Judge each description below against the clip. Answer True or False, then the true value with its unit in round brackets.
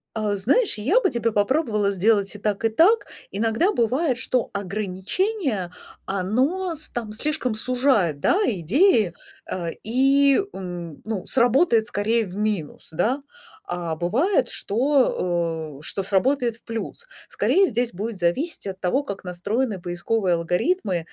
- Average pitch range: False (6.1 semitones)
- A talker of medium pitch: False (220 Hz)